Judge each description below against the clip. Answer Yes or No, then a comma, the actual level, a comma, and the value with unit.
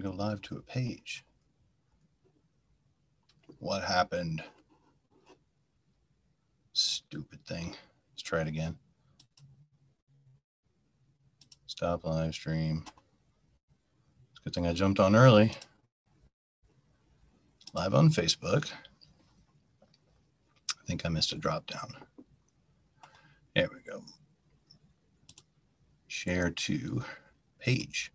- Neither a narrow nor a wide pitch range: No, wide, 8.4 semitones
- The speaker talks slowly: Yes, slow, 85 wpm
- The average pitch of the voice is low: Yes, low, 120 Hz